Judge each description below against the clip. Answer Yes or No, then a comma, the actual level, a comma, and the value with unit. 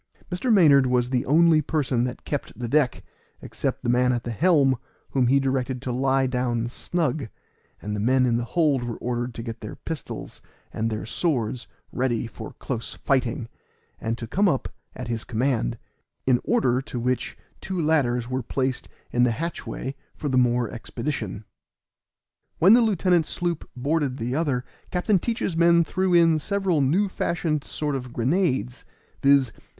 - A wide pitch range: No, average, 4.8 semitones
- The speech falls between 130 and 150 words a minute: No, average, 165 wpm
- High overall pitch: No, low, 130 Hz